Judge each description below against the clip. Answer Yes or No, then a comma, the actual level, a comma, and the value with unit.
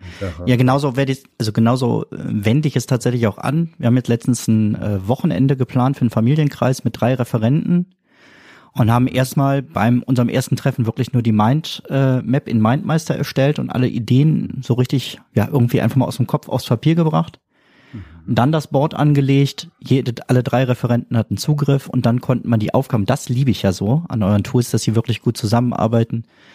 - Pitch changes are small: No, average, 3.0 semitones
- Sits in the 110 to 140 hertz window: Yes, low, 125 Hz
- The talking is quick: Yes, fast, 195 wpm